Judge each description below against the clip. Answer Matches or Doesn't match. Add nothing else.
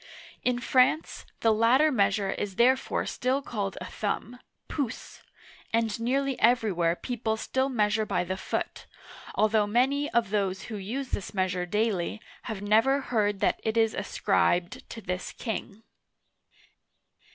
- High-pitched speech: Matches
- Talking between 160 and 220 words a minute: Doesn't match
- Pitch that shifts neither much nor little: Matches